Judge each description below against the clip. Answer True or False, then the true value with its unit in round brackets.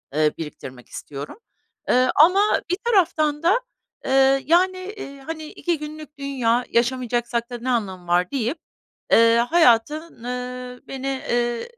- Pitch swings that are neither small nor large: True (4.7 semitones)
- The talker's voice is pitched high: True (255 Hz)